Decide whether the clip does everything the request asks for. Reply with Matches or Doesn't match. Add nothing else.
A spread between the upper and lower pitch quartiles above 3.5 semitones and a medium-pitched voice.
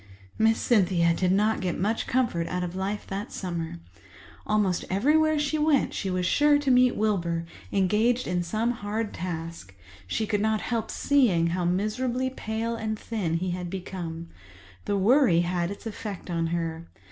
Doesn't match